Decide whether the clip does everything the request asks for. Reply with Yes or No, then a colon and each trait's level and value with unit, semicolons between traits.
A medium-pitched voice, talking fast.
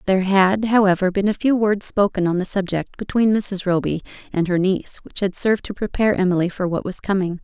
No: high, 195 Hz; fast, 220 wpm